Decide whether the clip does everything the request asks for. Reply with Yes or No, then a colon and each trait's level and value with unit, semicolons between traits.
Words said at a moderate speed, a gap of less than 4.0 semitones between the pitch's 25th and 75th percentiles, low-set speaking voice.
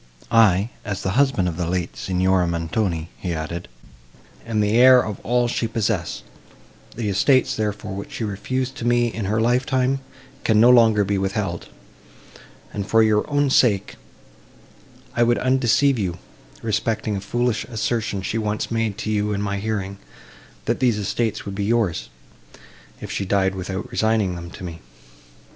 Yes: average, 160 wpm; average, 3.5 semitones; low, 105 Hz